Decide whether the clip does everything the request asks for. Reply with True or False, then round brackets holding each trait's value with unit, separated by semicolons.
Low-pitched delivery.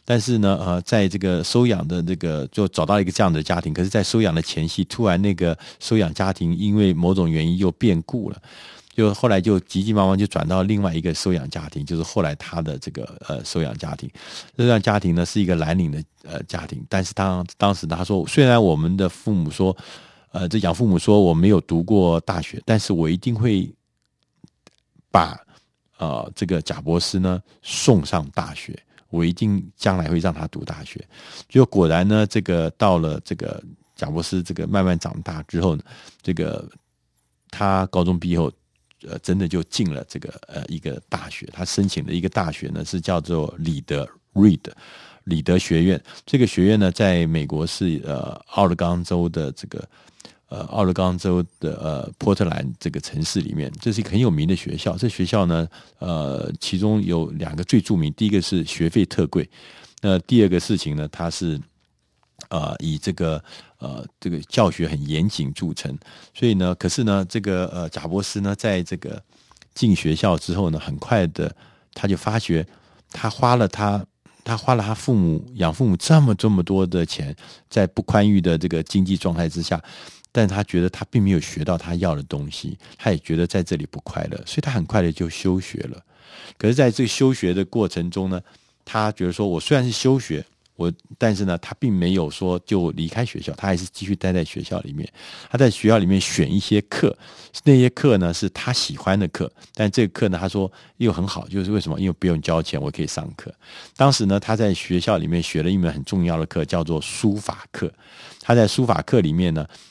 True (95 Hz)